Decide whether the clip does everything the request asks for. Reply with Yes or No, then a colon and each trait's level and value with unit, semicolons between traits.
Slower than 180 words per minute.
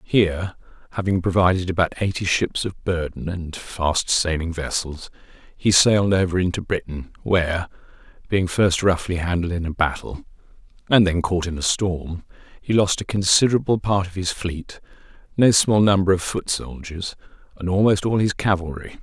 Yes: average, 160 wpm